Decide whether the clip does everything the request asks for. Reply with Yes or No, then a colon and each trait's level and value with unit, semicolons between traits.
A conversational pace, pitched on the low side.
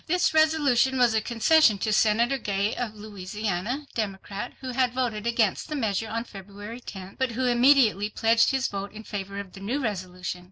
No: average, 185 wpm; high, 220 Hz